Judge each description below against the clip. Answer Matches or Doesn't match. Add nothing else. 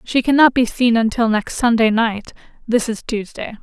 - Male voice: Doesn't match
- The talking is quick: Doesn't match